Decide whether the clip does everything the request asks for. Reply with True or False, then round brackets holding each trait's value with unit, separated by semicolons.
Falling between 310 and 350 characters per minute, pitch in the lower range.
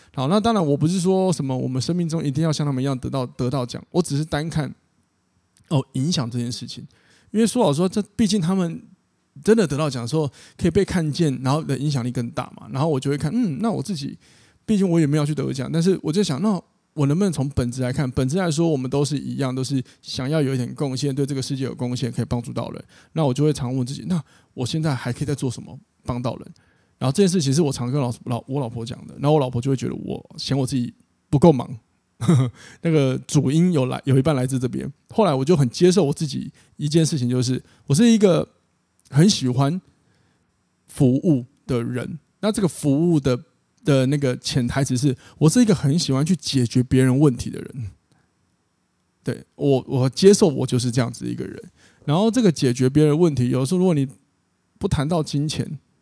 False (325 characters per minute; 145 Hz)